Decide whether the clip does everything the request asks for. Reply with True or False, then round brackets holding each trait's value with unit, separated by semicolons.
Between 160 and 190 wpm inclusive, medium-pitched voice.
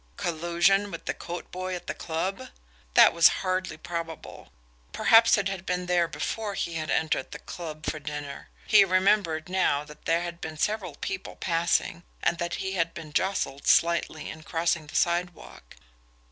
True (170 wpm; 170 Hz)